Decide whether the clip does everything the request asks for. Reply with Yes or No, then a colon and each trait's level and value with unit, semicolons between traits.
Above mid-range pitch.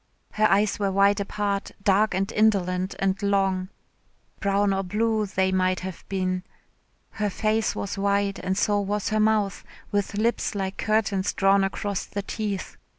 Yes: high, 200 Hz